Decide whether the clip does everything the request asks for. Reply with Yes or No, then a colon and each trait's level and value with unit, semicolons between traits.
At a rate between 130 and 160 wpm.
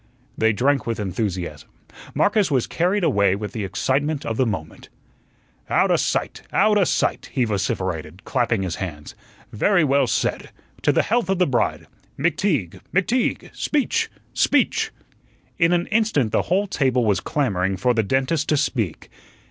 Yes: average, 150 wpm